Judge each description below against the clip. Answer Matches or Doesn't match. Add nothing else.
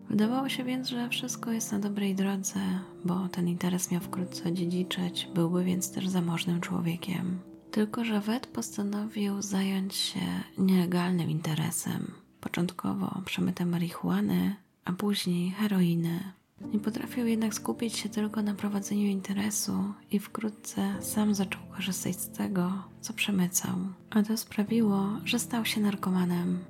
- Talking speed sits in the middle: Matches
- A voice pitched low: Doesn't match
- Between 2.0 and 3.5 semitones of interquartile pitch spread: Matches